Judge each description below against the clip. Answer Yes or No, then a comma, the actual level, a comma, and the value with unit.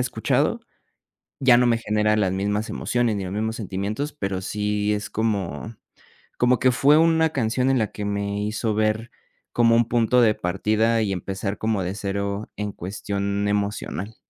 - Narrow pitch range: Yes, narrow, 2.3 semitones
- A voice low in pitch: Yes, low, 105 Hz